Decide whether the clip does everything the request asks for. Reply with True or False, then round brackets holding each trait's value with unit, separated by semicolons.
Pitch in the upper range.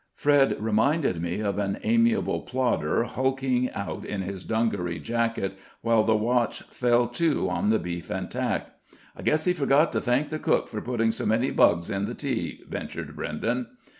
False (115 Hz)